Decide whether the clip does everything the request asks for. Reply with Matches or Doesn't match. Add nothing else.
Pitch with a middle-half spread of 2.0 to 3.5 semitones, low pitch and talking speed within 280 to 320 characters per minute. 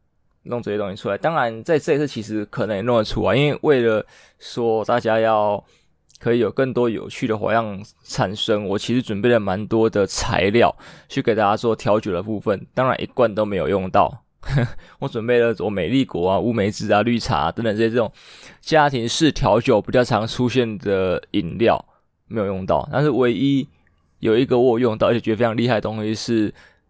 Matches